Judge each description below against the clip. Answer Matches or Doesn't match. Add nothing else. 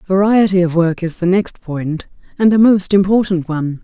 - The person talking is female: Matches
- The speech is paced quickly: Doesn't match